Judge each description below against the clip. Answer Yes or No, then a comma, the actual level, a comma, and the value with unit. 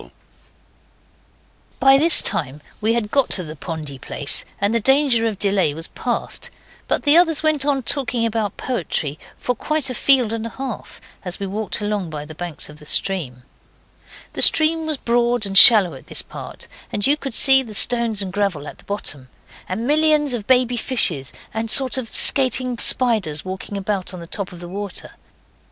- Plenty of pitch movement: Yes, wide, 5.9 semitones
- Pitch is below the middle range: No, high, 220 Hz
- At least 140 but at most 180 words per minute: No, average, 190 wpm